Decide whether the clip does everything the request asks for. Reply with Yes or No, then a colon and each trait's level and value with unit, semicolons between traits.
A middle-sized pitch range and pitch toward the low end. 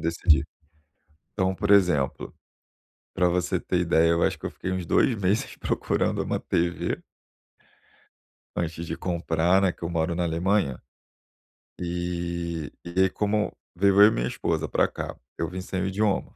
No: narrow, 2.1 semitones; very low, 90 Hz